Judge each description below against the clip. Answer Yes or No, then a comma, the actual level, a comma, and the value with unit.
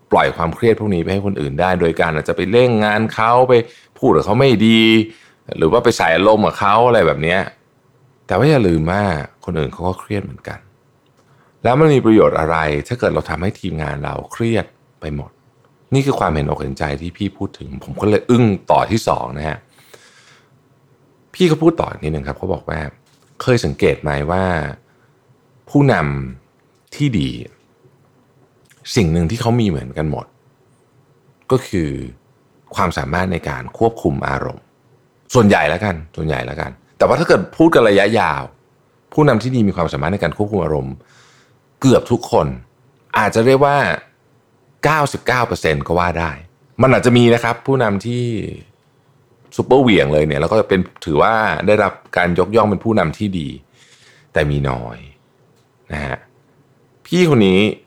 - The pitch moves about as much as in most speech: No, wide, 8.2 semitones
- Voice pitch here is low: Yes, low, 105 Hz